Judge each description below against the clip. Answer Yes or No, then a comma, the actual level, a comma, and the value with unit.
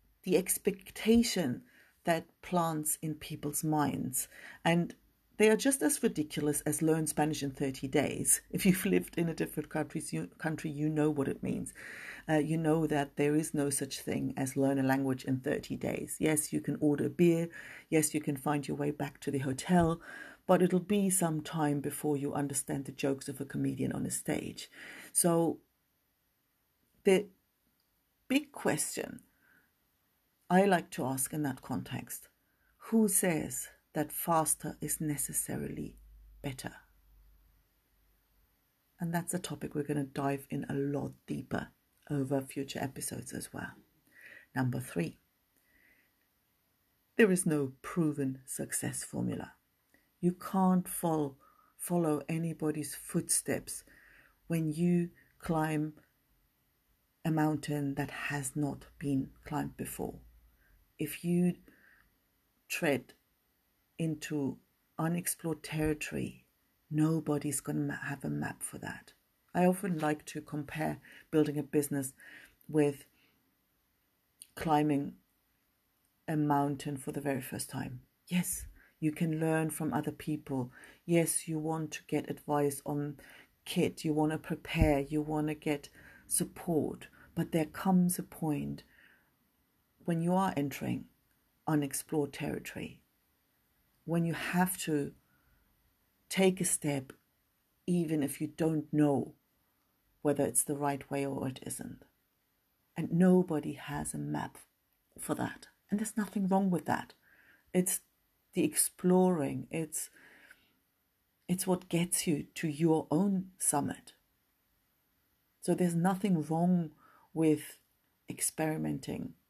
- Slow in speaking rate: Yes, slow, 130 wpm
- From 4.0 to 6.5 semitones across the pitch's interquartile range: No, average, 3.0 semitones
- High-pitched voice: No, medium, 150 Hz